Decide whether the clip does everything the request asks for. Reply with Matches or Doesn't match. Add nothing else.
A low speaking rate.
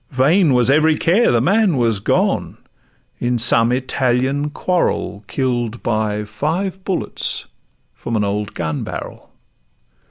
Matches